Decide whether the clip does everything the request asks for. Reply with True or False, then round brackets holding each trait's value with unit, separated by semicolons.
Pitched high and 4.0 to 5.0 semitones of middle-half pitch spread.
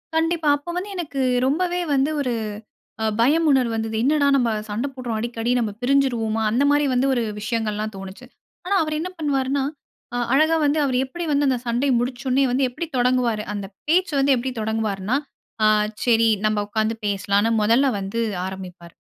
True (250 Hz; 4.4 semitones)